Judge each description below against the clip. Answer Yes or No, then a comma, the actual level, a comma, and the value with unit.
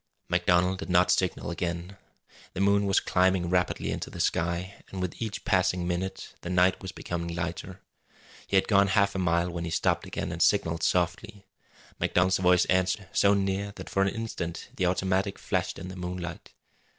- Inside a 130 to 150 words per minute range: No, average, 180 wpm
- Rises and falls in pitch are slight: Yes, narrow, 1.8 semitones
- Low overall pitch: Yes, very low, 90 Hz